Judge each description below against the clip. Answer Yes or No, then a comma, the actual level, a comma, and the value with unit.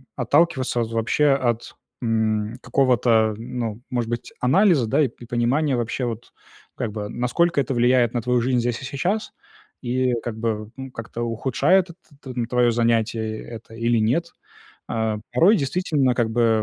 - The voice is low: Yes, low, 120 Hz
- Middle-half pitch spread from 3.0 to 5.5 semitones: No, narrow, 2.6 semitones